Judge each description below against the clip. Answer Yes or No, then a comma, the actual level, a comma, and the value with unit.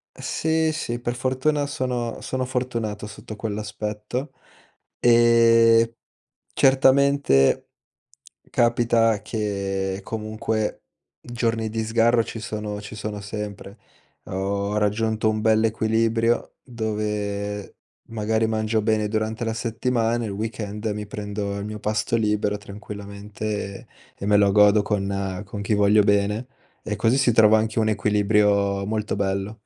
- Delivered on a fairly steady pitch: Yes, narrow, 1.8 semitones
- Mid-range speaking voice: No, low, 110 Hz